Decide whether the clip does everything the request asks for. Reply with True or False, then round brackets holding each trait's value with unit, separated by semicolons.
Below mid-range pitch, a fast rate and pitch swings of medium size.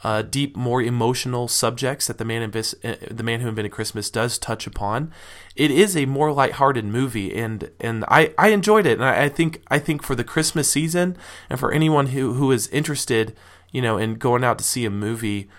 True (120 Hz; 220 wpm; 4.3 semitones)